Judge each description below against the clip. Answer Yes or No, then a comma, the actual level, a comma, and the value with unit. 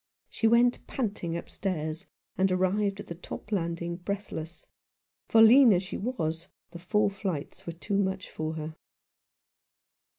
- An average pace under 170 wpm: Yes, average, 140 wpm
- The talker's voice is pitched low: No, medium, 185 Hz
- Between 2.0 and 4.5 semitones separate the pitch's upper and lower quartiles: Yes, average, 3.5 semitones